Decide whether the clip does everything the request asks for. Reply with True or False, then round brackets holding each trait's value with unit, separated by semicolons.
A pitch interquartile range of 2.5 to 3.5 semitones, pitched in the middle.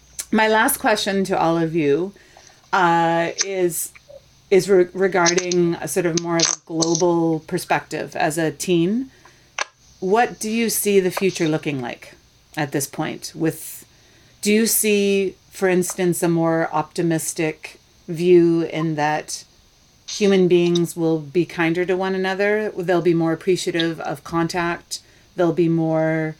True (2.8 semitones; 170 Hz)